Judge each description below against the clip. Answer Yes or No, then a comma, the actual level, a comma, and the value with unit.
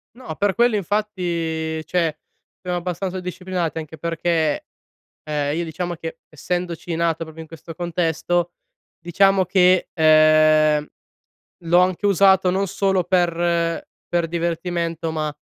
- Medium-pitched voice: Yes, medium, 170 Hz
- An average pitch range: No, narrow, 2.2 semitones